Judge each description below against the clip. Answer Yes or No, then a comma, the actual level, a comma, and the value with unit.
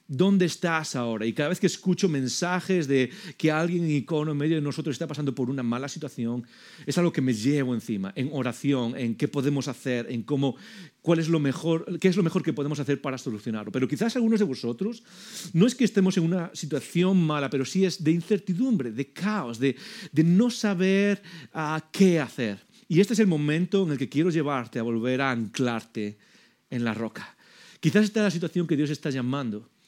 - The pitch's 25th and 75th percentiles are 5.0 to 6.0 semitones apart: Yes, wide, 5.6 semitones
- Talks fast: Yes, fast, 210 wpm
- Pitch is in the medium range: Yes, medium, 155 Hz